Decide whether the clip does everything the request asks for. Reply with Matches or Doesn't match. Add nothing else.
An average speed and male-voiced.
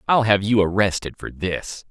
Matches